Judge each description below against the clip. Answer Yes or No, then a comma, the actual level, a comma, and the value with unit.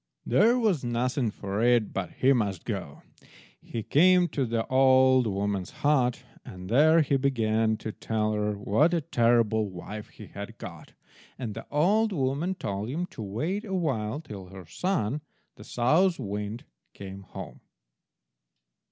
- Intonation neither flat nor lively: No, wide, 5.9 semitones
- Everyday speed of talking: Yes, average, 150 wpm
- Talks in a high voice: No, low, 120 Hz